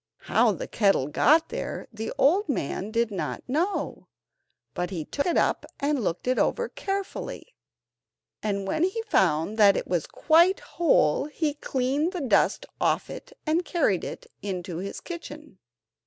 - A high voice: Yes, very high, 270 Hz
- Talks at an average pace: Yes, average, 155 wpm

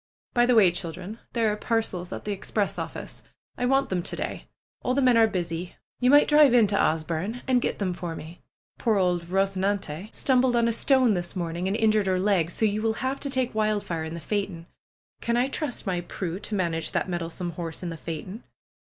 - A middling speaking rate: No, fast, 215 wpm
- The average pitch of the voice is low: No, high, 200 Hz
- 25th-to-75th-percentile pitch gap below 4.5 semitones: No, average, 5.0 semitones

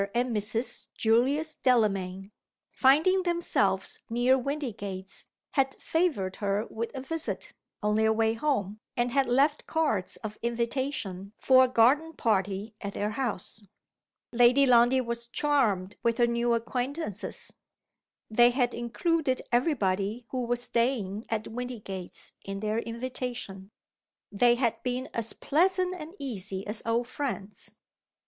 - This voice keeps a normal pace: No, slow, 130 wpm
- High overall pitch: Yes, high, 235 Hz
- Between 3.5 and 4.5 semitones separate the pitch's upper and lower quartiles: Yes, average, 3.9 semitones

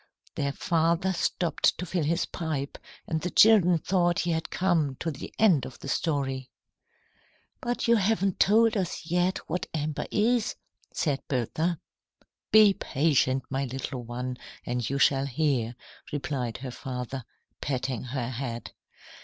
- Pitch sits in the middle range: Yes, medium, 150 Hz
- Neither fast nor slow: Yes, average, 145 wpm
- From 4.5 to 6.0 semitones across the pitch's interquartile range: Yes, average, 5.2 semitones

